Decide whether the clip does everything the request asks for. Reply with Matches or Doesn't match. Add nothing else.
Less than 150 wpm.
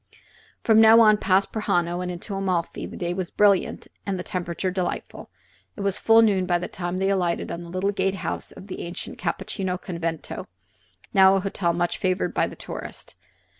Doesn't match